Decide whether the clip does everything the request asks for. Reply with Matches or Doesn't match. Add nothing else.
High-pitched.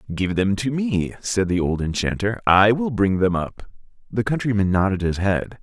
Doesn't match